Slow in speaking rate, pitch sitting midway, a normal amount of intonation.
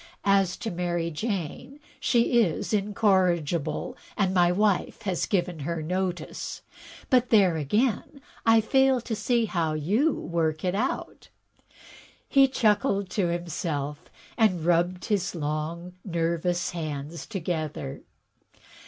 Yes: slow, 120 wpm; medium, 180 Hz; average, 4.3 semitones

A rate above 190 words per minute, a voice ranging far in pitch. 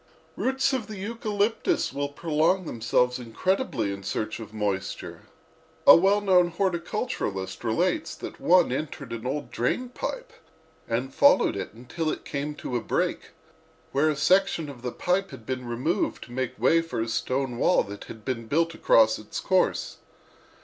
No: average, 165 wpm; wide, 7.9 semitones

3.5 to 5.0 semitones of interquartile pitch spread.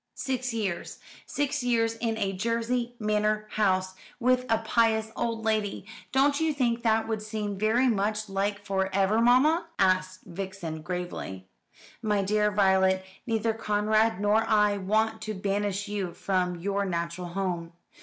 No: average, 3.0 semitones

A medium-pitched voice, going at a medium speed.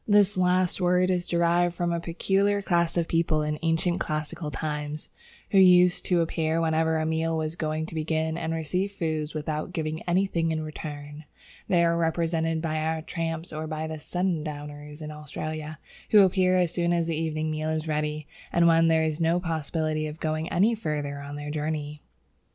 Yes: medium, 160 Hz; average, 185 wpm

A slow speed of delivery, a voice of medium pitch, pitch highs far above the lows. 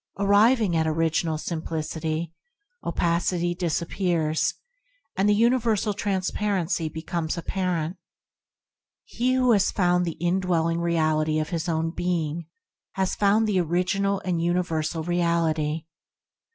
No: slow, 110 wpm; medium, 175 Hz; average, 3.1 semitones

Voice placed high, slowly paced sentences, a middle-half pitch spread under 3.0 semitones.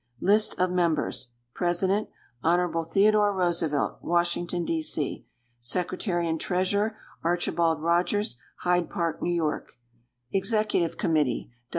No: medium, 175 Hz; slow, 105 wpm; narrow, 2.4 semitones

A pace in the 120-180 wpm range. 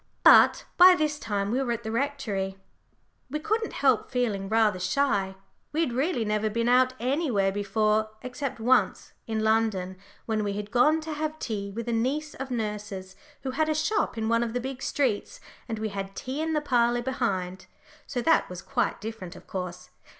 No: average, 190 wpm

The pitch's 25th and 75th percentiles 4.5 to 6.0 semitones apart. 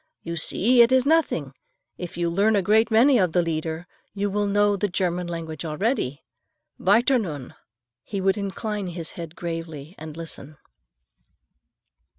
No: average, 4.1 semitones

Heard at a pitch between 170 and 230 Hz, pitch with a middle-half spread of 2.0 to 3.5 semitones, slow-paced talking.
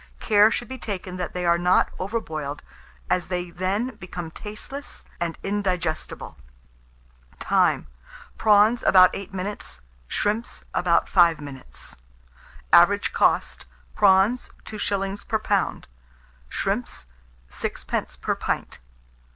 Yes: high, 190 Hz; average, 3.1 semitones; slow, 110 wpm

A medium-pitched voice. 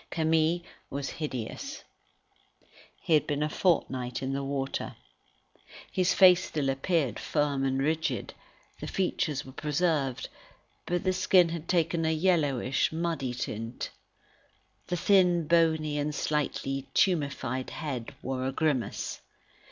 Yes: medium, 150 Hz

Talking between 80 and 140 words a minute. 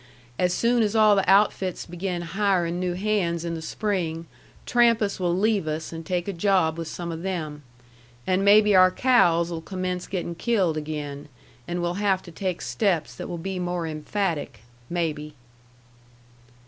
No: average, 160 wpm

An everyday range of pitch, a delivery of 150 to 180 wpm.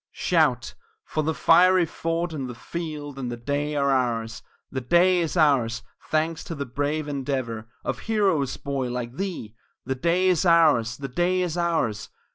Yes: average, 5.0 semitones; average, 170 wpm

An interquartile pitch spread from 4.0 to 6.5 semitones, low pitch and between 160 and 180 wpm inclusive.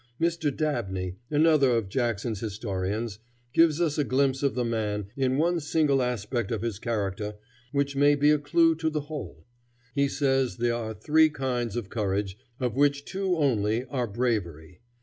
Yes: average, 5.3 semitones; low, 125 Hz; average, 170 wpm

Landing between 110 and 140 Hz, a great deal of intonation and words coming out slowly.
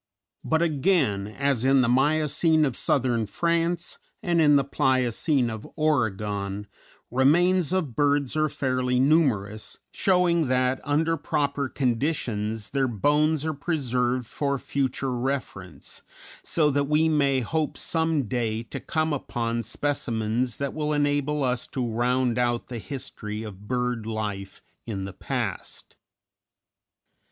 No: low, 135 Hz; average, 4.4 semitones; slow, 130 wpm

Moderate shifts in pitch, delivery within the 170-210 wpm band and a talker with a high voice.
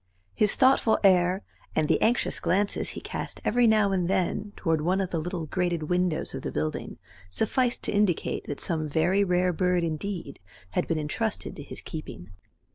No: average, 4.0 semitones; average, 180 wpm; medium, 180 Hz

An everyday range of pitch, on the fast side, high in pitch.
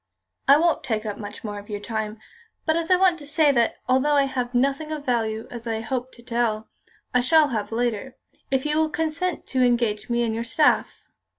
Yes: average, 4.9 semitones; fast, 210 wpm; very high, 250 Hz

